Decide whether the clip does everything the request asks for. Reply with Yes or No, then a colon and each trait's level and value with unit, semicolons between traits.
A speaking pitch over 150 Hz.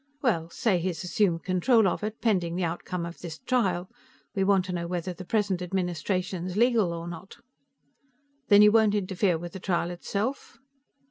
Yes: medium, 185 Hz